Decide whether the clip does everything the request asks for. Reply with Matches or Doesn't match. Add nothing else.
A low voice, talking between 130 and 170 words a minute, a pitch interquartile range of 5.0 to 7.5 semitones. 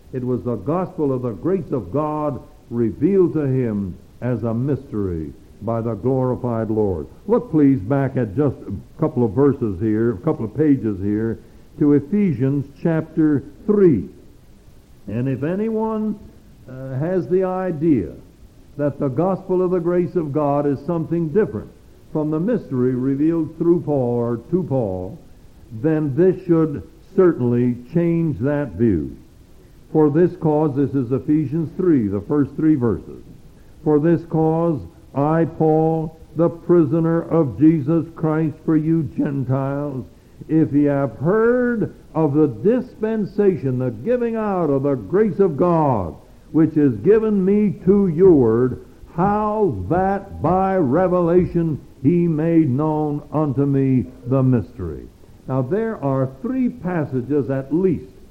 Doesn't match